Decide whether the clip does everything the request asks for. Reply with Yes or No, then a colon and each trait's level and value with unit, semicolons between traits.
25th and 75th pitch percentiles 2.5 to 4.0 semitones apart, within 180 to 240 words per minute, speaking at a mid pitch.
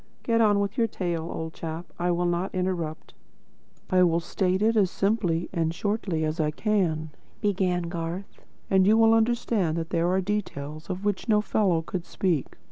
Yes: average, 3.7 semitones; average, 185 wpm; medium, 180 Hz